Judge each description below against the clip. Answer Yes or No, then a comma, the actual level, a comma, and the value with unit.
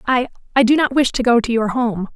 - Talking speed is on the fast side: Yes, fast, 250 wpm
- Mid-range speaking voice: No, high, 240 Hz